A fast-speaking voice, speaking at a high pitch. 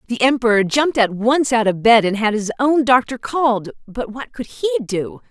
Yes: fast, 215 wpm; high, 240 Hz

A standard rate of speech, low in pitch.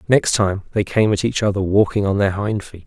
No: fast, 250 wpm; low, 100 Hz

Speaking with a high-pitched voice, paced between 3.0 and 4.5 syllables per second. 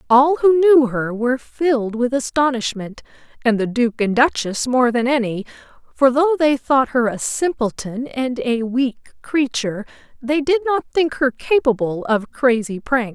Yes: very high, 255 Hz; 4.4 syllables/s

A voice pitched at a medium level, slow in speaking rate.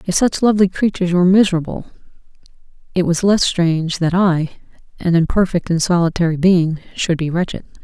No: medium, 175 Hz; average, 155 wpm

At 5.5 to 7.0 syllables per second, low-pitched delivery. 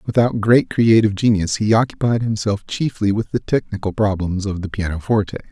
Yes: 5.6 syllables/s; low, 105 Hz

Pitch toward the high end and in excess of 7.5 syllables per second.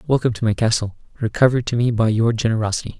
No: low, 115 Hz; 7.7 syllables/s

